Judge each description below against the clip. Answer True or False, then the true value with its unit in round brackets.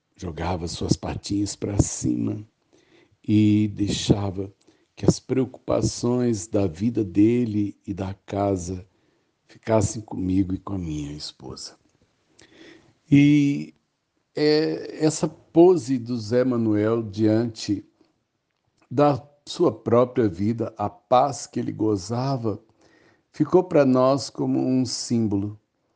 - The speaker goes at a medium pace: False (105 wpm)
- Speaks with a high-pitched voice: False (110 Hz)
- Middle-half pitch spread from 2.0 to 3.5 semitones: False (4.0 semitones)